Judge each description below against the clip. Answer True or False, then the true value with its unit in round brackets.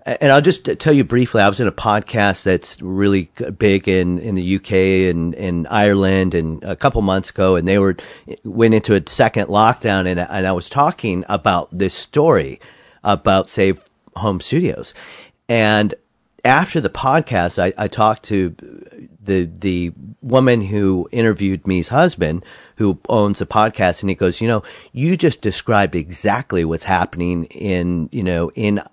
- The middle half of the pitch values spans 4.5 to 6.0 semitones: False (3.2 semitones)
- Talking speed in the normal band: True (165 wpm)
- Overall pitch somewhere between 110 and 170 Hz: False (100 Hz)